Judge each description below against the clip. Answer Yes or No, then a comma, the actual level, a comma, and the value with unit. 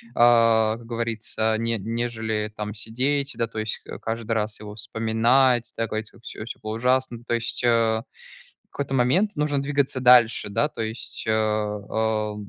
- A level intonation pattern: Yes, narrow, 2.0 semitones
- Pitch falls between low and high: No, low, 115 Hz